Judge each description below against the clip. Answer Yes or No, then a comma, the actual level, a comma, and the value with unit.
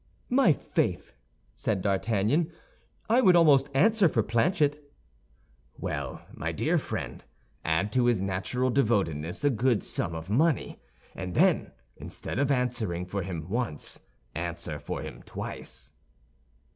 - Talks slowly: Yes, slow, 130 wpm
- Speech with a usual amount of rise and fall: No, wide, 7.8 semitones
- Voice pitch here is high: No, low, 115 Hz